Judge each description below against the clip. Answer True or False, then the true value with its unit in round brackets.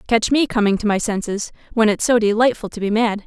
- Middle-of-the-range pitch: False (220 Hz)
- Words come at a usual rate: False (240 wpm)